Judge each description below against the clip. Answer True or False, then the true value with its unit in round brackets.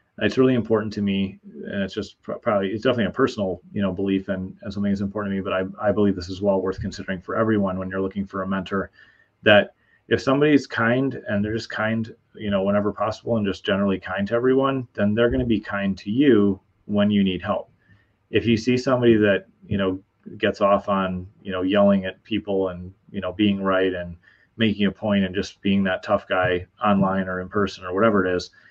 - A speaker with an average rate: False (225 wpm)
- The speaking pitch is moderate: False (100 Hz)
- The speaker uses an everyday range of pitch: False (2.2 semitones)